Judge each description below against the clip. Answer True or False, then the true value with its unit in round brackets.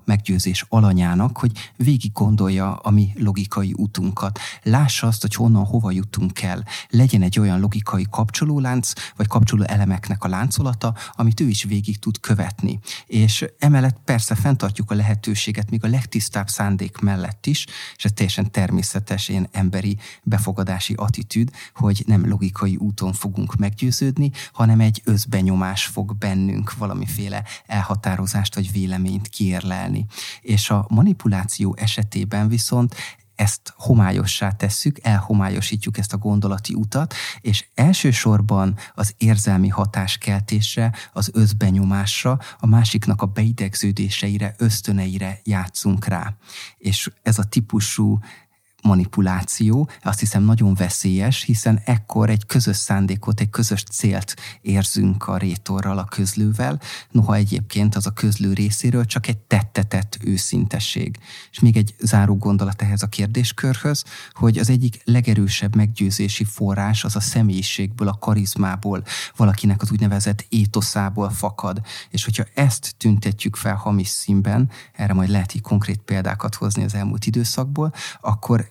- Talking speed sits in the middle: True (130 wpm)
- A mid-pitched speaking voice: False (105 Hz)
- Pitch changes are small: True (2.2 semitones)